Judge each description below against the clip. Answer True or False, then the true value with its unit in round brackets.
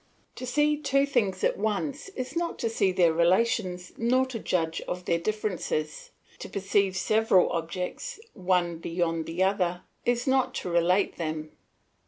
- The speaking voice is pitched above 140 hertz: True (190 Hz)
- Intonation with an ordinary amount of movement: False (5.9 semitones)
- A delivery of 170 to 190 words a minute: False (155 wpm)